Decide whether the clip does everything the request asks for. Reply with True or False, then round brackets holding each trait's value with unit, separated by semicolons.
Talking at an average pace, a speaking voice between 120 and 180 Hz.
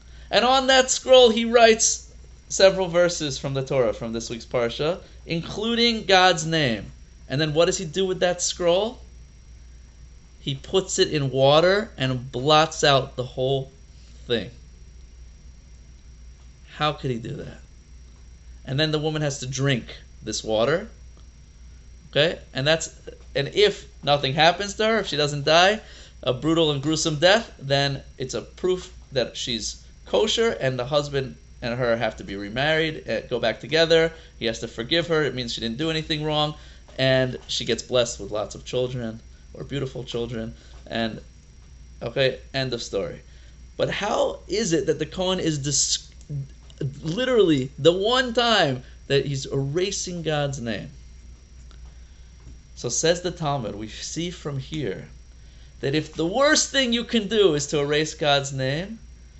True (160 wpm; 135 Hz)